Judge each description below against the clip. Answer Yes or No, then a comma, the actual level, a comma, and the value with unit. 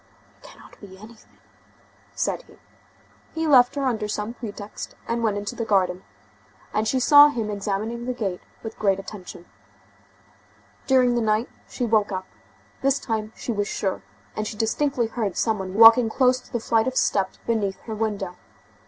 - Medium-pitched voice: No, high, 220 Hz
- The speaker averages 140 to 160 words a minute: No, average, 170 wpm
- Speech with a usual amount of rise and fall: Yes, average, 3.0 semitones